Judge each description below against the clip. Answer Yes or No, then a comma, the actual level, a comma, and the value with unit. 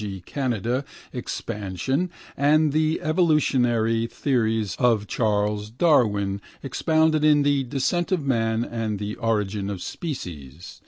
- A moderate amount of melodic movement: No, wide, 5.7 semitones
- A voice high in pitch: No, low, 120 Hz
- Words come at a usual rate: No, slow, 115 wpm